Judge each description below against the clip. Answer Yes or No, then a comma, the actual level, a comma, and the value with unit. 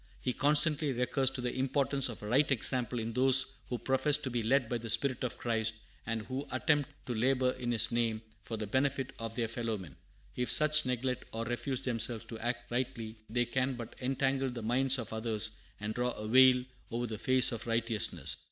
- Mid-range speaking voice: No, low, 125 Hz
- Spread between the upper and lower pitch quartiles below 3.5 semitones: Yes, narrow, 2.6 semitones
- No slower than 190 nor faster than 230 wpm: Yes, fast, 205 wpm